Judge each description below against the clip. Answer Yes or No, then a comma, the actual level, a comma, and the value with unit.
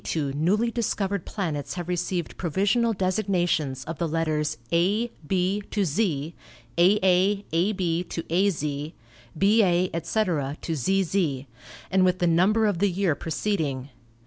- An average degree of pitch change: Yes, average, 3.6 semitones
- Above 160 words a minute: No, average, 140 wpm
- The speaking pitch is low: No, medium, 180 Hz